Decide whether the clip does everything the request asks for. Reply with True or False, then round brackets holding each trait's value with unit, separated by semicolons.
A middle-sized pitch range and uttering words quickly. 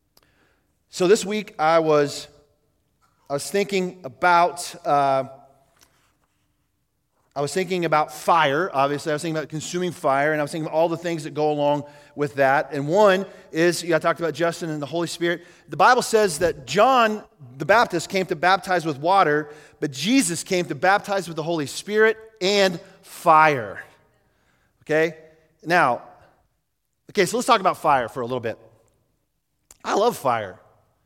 False (4.0 semitones; 165 wpm)